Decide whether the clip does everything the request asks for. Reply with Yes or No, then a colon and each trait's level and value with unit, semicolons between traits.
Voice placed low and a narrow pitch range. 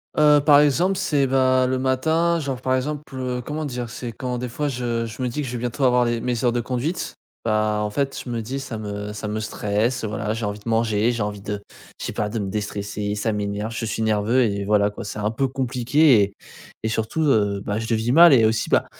No: low, 120 Hz; average, 3.6 semitones